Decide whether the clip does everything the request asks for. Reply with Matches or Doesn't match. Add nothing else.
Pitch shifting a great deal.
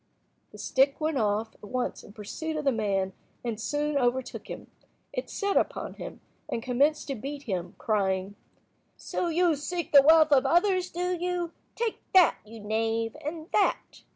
Matches